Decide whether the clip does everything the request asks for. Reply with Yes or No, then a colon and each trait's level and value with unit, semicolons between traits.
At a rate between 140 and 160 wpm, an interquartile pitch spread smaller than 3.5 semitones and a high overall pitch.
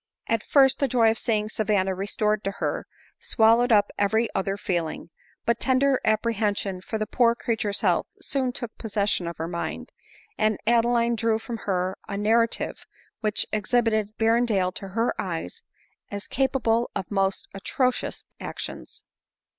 Yes: average, 150 wpm; average, 2.9 semitones; high, 215 Hz